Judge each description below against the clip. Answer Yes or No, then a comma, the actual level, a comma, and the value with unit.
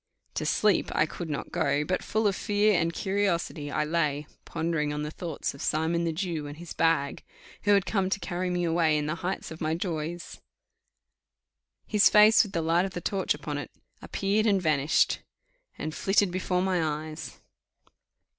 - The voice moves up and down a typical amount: Yes, average, 3.7 semitones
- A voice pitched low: No, medium, 170 Hz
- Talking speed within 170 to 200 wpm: Yes, average, 185 wpm